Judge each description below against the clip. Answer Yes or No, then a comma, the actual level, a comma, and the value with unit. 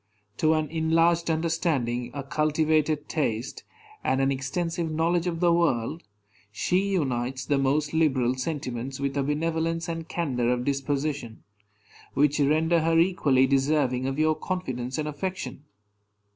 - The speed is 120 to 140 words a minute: Yes, slow, 135 wpm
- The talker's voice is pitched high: No, medium, 150 Hz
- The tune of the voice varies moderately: Yes, average, 3.6 semitones